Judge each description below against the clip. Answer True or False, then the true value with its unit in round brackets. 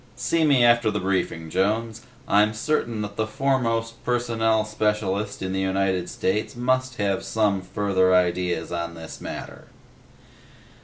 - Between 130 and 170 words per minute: True (140 wpm)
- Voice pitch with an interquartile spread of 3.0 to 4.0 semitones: True (3.5 semitones)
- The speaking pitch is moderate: False (105 Hz)